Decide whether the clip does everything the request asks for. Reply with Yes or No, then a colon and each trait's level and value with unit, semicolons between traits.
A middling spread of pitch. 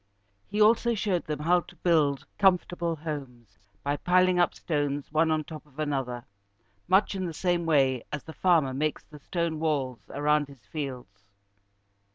Yes: average, 3.9 semitones